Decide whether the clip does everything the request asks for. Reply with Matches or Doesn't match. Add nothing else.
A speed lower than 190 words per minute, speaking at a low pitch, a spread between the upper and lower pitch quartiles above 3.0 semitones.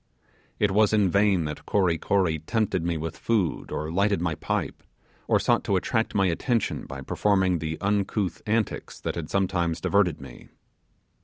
Matches